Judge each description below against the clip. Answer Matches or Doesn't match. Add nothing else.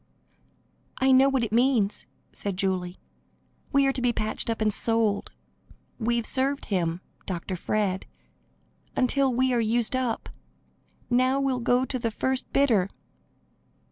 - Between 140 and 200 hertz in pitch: Doesn't match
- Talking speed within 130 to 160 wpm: Matches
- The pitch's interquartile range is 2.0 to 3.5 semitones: Doesn't match